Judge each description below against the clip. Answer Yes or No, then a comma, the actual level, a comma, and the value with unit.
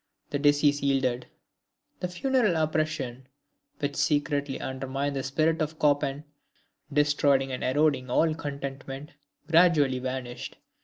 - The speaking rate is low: Yes, slow, 110 wpm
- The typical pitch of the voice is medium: Yes, medium, 145 Hz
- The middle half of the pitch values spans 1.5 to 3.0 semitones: Yes, narrow, 2.5 semitones